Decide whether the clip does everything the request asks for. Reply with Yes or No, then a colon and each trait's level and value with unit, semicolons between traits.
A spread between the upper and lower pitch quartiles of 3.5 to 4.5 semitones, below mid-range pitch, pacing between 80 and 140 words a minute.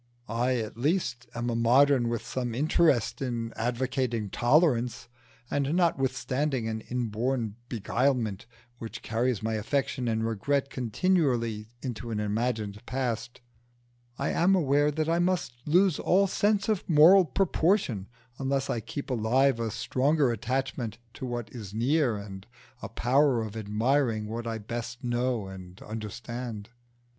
Yes: average, 3.8 semitones; low, 120 Hz; slow, 135 wpm